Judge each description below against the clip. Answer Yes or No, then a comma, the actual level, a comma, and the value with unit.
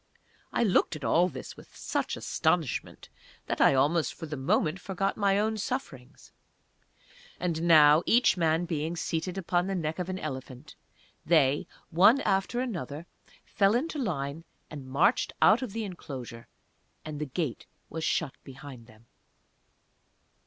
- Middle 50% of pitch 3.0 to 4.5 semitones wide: No, average, 5.2 semitones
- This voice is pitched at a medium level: Yes, medium, 165 Hz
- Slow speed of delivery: No, average, 145 wpm